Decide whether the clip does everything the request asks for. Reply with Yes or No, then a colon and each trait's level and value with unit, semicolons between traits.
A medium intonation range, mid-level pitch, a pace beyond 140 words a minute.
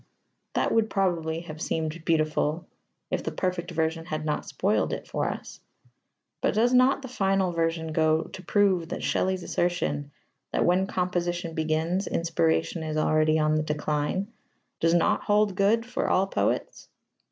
Yes: average, 3.2 semitones; medium, 170 Hz; average, 155 wpm